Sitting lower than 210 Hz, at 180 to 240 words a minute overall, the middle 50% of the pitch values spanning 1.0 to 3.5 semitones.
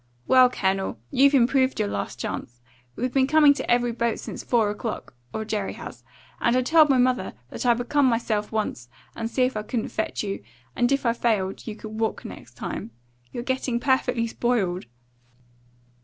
No: high, 235 Hz; average, 185 wpm; average, 3.2 semitones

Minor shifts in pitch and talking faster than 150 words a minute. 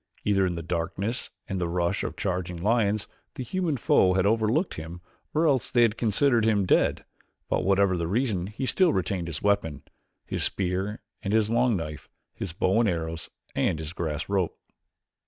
No: average, 4.6 semitones; average, 185 wpm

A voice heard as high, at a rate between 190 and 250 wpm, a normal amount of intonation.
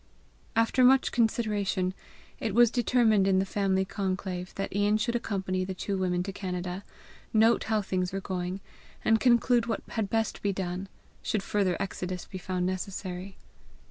No: high, 195 Hz; average, 160 wpm; average, 3.0 semitones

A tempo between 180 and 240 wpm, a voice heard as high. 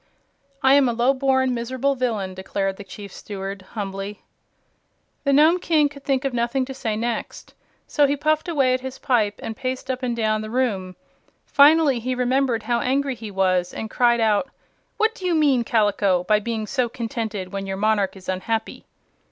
Yes: average, 185 wpm; high, 235 Hz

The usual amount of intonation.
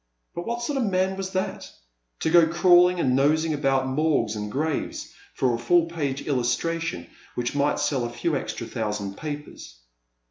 No: wide, 5.8 semitones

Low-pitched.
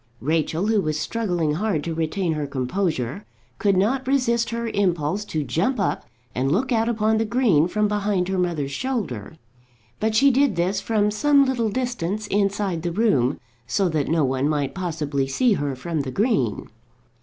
No: high, 190 Hz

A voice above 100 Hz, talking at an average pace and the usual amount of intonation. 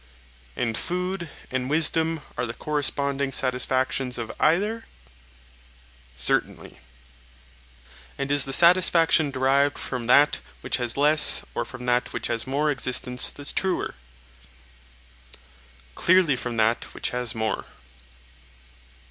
No: medium, 140 Hz; slow, 115 wpm; average, 4.0 semitones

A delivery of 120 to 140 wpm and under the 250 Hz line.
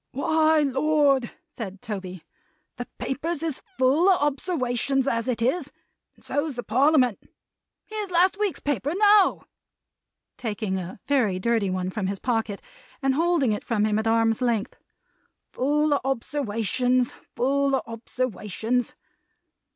No: slow, 135 wpm; very high, 255 Hz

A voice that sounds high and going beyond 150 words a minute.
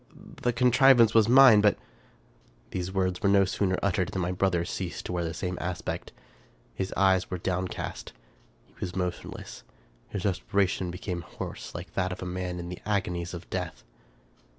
No: very low, 95 Hz; average, 175 wpm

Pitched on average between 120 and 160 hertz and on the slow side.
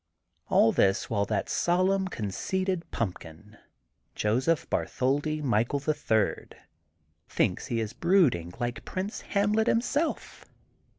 Yes: medium, 140 Hz; slow, 120 wpm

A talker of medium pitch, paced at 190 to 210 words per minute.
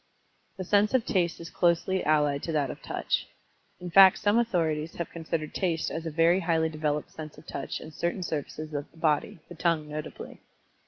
Yes: medium, 165 Hz; average, 195 wpm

